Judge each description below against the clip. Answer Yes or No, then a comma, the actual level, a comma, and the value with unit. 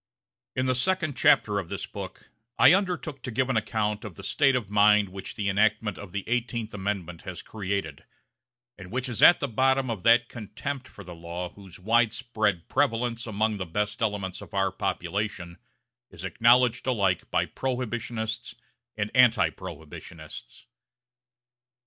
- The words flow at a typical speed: Yes, average, 155 wpm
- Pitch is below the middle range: Yes, low, 110 Hz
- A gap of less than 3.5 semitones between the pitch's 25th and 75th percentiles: No, average, 3.9 semitones